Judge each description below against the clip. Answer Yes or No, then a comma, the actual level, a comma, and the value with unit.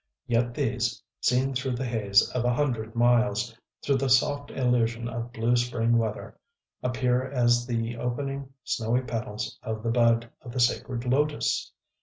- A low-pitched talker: Yes, low, 120 Hz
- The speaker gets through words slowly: No, average, 155 wpm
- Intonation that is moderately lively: No, narrow, 1.6 semitones